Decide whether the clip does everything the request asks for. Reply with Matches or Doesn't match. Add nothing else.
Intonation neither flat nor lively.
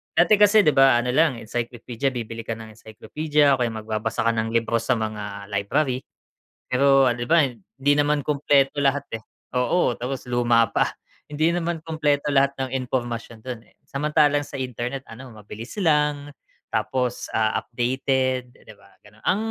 Matches